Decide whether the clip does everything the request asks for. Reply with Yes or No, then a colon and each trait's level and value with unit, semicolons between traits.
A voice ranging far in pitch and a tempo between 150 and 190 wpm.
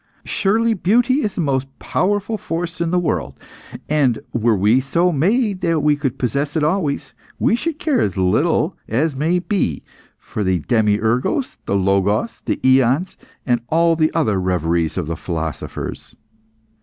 Yes: wide, 8.9 semitones; average, 155 wpm